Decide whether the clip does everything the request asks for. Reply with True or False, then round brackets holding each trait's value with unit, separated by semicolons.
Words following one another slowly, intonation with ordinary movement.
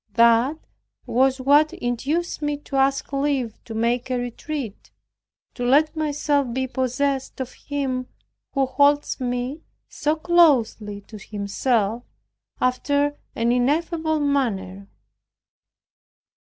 True (110 wpm; 3.3 semitones)